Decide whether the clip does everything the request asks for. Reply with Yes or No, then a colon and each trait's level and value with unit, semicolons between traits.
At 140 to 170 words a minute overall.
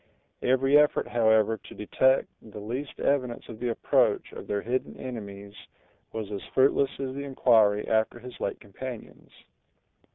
Yes: average, 150 wpm